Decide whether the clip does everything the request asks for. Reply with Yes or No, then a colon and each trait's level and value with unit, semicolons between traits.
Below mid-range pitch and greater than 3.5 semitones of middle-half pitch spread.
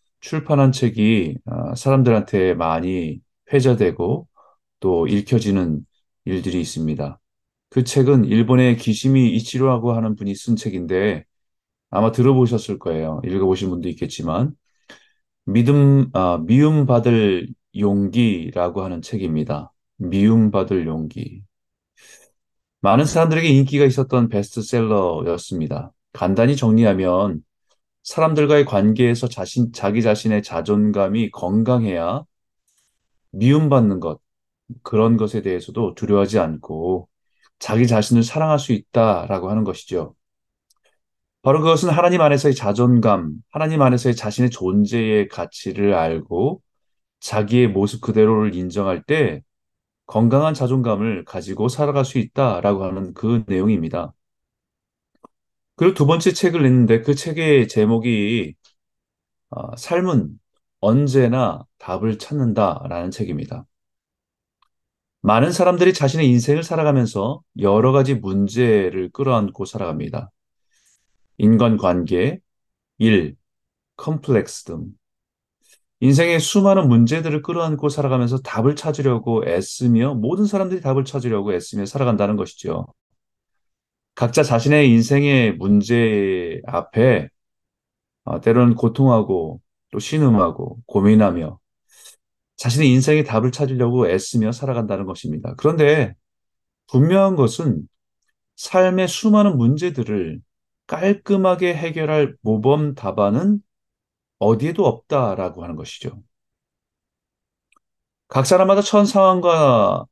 Yes: low, 120 Hz; wide, 5.4 semitones